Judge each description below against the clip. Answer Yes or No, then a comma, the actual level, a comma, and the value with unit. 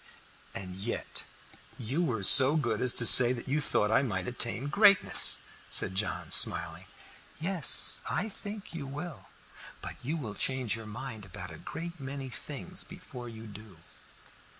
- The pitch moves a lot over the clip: Yes, wide, 6.0 semitones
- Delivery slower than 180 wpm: Yes, average, 155 wpm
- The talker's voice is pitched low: Yes, low, 130 Hz